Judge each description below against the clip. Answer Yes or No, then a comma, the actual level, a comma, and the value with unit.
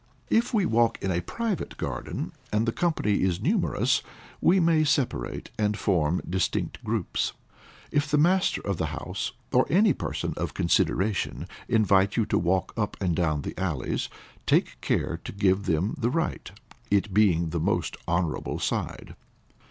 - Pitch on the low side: Yes, low, 100 Hz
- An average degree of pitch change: No, wide, 8.7 semitones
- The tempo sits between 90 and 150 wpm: No, average, 160 wpm